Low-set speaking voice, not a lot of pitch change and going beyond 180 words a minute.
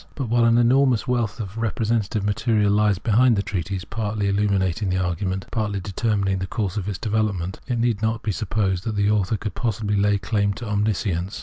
Yes: low, 105 Hz; narrow, 2.3 semitones; average, 200 wpm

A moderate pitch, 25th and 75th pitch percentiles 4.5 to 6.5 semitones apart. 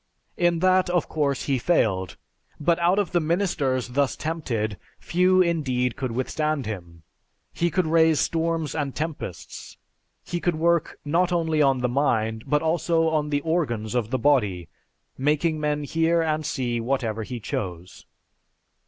Yes: medium, 150 Hz; average, 5.1 semitones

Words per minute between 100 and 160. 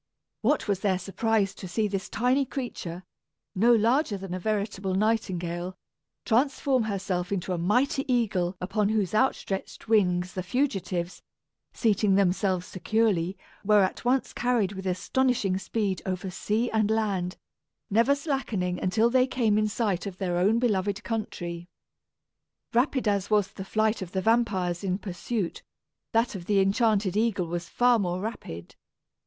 Yes: average, 150 wpm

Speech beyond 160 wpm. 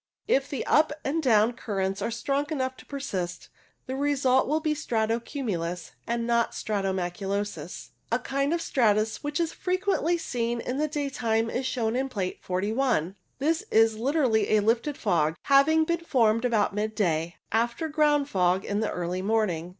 Yes: average, 170 wpm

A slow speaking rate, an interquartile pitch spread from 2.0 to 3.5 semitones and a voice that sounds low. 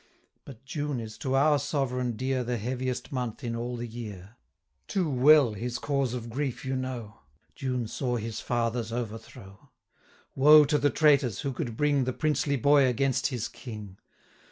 No: average, 170 wpm; average, 3.0 semitones; low, 125 Hz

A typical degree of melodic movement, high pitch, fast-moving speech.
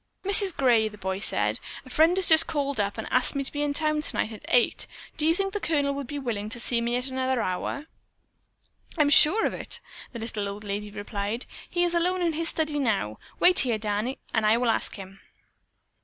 No: wide, 6.3 semitones; very high, 255 Hz; fast, 220 wpm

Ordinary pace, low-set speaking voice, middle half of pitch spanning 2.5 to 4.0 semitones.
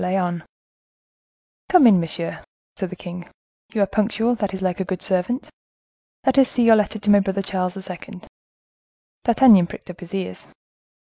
No: average, 170 wpm; high, 195 Hz; average, 3.3 semitones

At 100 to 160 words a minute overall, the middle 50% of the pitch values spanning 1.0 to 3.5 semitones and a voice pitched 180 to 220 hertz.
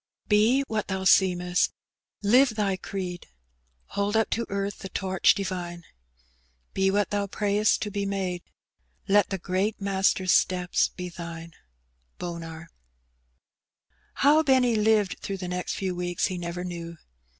Yes: slow, 135 wpm; narrow, 2.6 semitones; high, 190 Hz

